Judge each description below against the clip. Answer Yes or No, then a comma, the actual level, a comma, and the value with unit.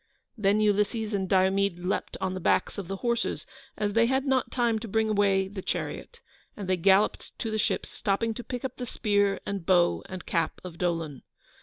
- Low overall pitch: No, high, 200 Hz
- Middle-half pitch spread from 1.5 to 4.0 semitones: Yes, average, 3.0 semitones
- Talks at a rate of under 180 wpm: No, average, 200 wpm